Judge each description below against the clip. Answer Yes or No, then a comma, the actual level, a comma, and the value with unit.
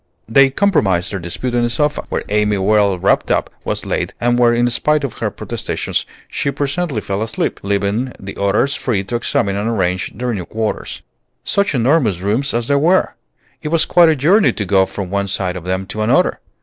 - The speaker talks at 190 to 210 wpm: Yes, average, 200 wpm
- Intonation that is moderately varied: No, wide, 5.8 semitones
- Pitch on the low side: Yes, low, 115 Hz